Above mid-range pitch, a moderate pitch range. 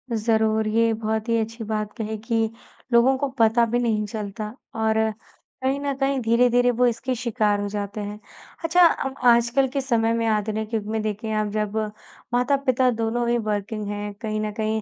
No: high, 225 Hz; narrow, 2.1 semitones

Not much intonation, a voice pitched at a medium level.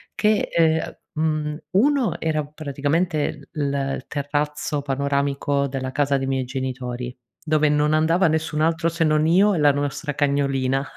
Yes: narrow, 2.3 semitones; medium, 150 Hz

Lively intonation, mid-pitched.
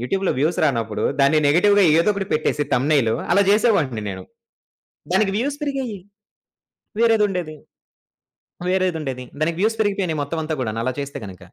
Yes: wide, 6.6 semitones; medium, 165 Hz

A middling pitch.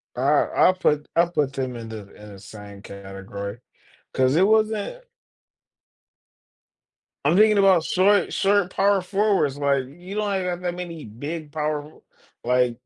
Yes: medium, 155 Hz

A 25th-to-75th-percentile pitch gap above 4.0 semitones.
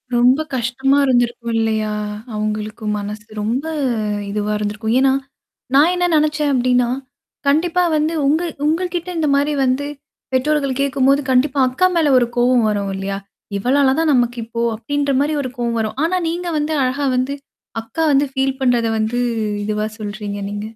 Yes: average, 4.6 semitones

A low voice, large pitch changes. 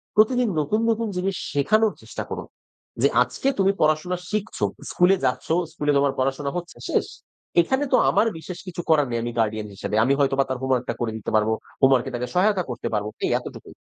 No: medium, 150 Hz; wide, 7.2 semitones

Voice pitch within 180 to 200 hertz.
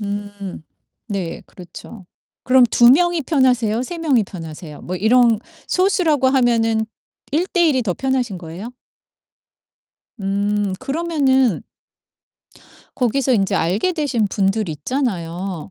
No: high, 225 Hz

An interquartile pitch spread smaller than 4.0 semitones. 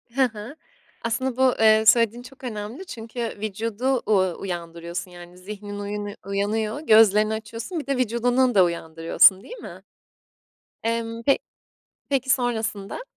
Yes: average, 3.4 semitones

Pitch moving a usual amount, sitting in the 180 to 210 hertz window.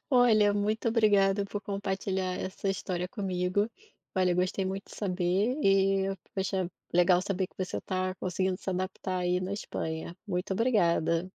No: narrow, 1.8 semitones; high, 190 Hz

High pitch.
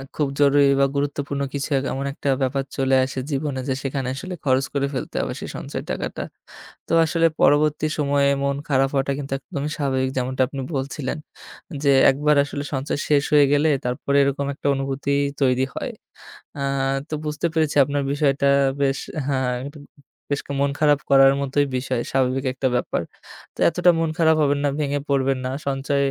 No: medium, 140 Hz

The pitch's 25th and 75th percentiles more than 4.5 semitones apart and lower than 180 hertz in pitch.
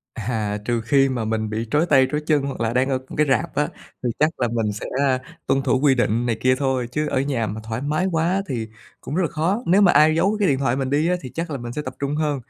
No: average, 4.2 semitones; low, 135 Hz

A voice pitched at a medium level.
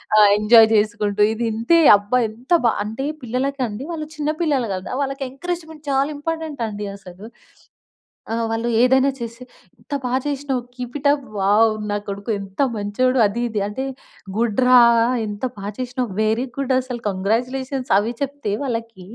No: high, 245 Hz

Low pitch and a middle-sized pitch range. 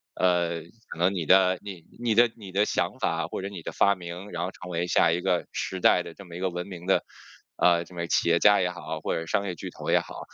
No: very low, 90 Hz; narrow, 2.1 semitones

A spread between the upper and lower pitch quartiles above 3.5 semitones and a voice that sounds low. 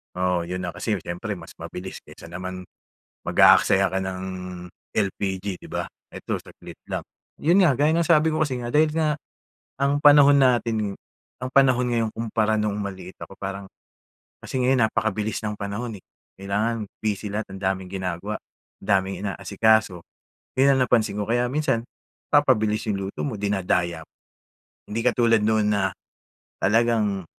Yes: average, 4.1 semitones; low, 105 Hz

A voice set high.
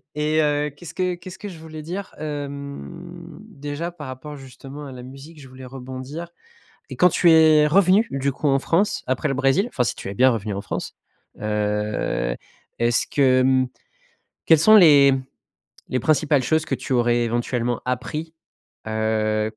No: medium, 140 Hz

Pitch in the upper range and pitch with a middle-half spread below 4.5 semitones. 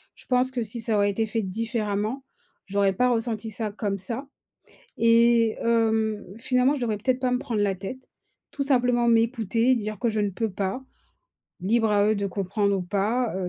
Yes: high, 225 Hz; average, 2.9 semitones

